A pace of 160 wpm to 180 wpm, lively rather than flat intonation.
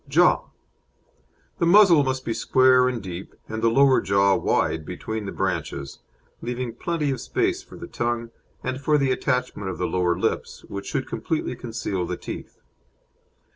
Yes: average, 165 wpm; wide, 5.9 semitones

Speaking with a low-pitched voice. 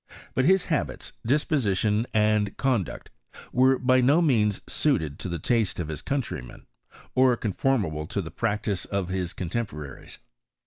Yes: low, 105 Hz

